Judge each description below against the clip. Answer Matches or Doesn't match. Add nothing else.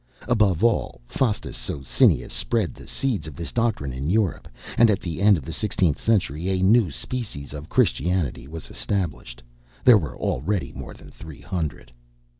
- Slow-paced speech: Doesn't match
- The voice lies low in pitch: Matches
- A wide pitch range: Matches